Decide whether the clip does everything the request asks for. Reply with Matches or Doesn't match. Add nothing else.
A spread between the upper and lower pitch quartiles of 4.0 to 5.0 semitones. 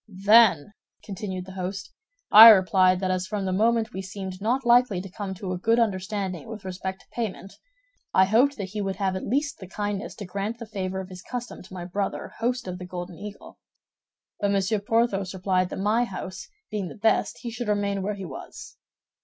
Doesn't match